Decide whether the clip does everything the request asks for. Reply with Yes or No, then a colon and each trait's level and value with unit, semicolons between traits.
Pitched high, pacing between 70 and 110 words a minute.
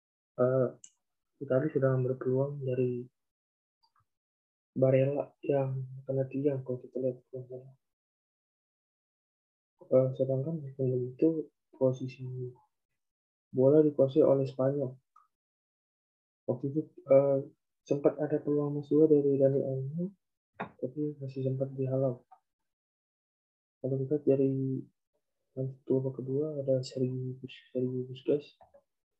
No: low, 130 Hz; average, 90 wpm